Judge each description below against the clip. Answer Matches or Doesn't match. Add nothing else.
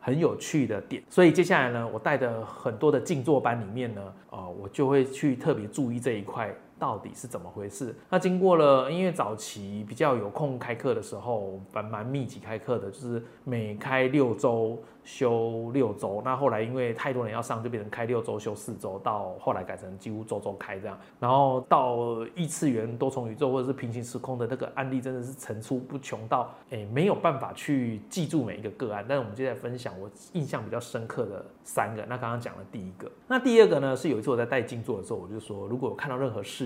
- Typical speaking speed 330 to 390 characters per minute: Matches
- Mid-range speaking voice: Doesn't match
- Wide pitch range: Doesn't match